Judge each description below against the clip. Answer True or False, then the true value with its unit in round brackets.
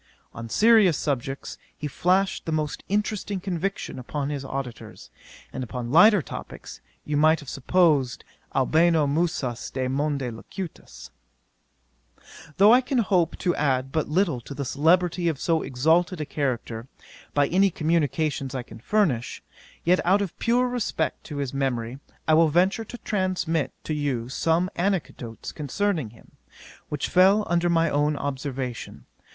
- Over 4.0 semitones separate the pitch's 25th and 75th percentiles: True (5.1 semitones)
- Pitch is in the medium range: True (155 Hz)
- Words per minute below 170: True (145 wpm)